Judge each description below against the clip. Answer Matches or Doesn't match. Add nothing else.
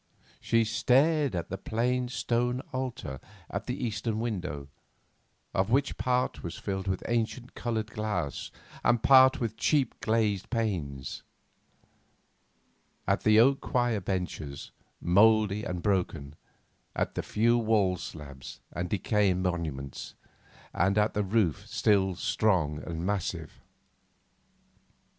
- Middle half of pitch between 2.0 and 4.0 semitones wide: Doesn't match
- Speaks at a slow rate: Matches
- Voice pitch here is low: Matches